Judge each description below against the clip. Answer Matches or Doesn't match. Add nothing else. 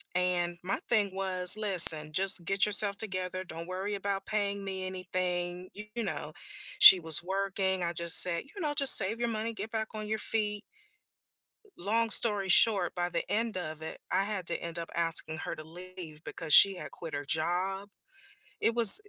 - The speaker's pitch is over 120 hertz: Matches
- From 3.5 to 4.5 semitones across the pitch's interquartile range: Doesn't match